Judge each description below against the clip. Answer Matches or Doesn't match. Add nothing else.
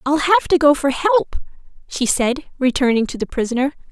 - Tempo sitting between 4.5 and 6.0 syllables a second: Matches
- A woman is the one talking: Matches